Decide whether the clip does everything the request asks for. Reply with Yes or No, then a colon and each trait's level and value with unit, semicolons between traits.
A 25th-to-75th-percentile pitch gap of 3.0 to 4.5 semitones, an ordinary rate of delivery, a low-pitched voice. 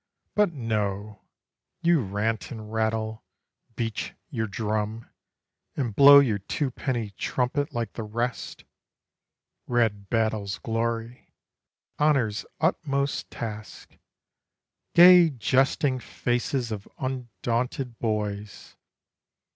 No: average, 3.4 semitones; slow, 90 wpm; low, 115 Hz